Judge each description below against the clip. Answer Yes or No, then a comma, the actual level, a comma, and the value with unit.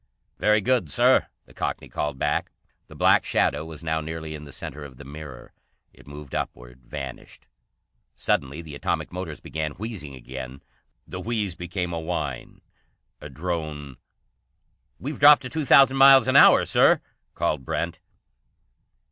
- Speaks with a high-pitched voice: No, very low, 80 Hz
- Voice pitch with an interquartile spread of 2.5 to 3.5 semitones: No, average, 5.0 semitones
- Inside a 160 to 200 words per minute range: No, average, 150 wpm